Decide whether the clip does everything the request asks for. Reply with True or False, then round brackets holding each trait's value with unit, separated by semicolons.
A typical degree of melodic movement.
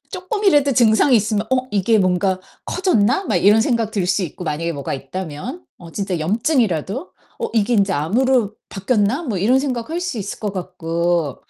False (6.0 semitones)